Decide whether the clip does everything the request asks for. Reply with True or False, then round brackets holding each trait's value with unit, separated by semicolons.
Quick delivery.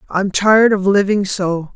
False (135 wpm)